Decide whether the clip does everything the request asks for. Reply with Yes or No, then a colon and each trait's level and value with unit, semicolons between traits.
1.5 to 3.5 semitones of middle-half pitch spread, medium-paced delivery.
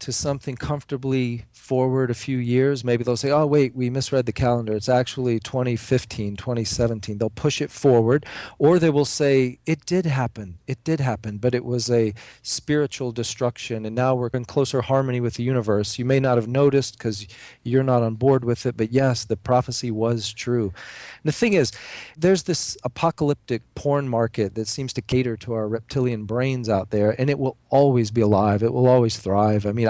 Yes: average, 2.9 semitones; average, 195 wpm